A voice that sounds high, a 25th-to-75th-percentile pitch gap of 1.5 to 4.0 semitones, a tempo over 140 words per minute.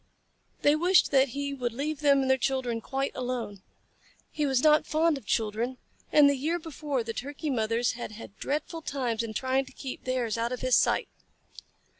Yes: very high, 265 Hz; average, 3.3 semitones; average, 190 wpm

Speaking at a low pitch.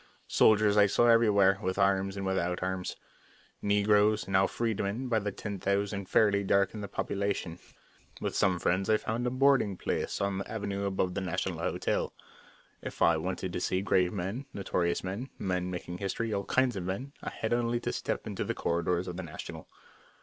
Yes: low, 100 Hz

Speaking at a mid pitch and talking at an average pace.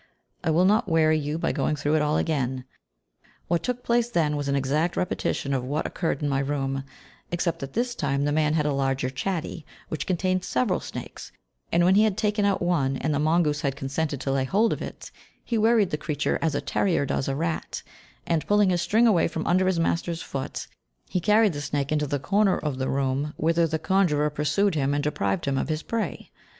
No: medium, 155 Hz; fast, 220 wpm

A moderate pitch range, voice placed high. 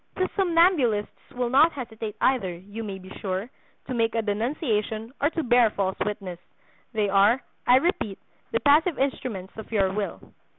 Yes: average, 4.6 semitones; high, 225 Hz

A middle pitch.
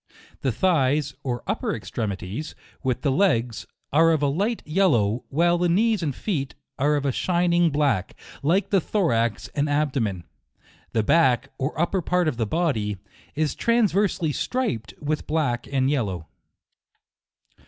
Yes: medium, 145 Hz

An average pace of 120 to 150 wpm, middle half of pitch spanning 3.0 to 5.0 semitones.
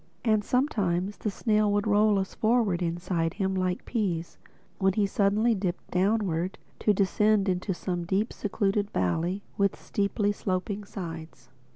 No: average, 145 wpm; narrow, 2.6 semitones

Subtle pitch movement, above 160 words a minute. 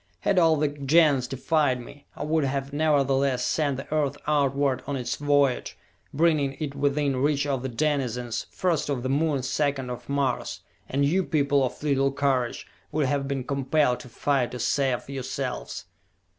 Yes: narrow, 1.9 semitones; average, 170 wpm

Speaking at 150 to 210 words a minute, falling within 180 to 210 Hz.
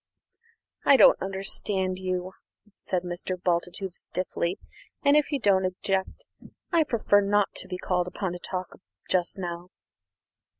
No: slow, 135 wpm; medium, 185 Hz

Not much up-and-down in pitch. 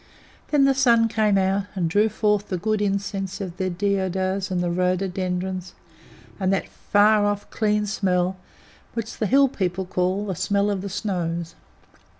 Yes: narrow, 2.2 semitones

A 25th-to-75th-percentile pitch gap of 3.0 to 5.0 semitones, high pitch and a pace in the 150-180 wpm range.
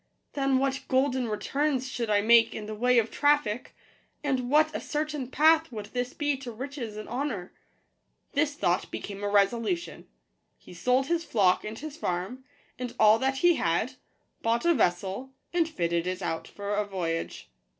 No: wide, 5.4 semitones; high, 245 Hz; average, 170 wpm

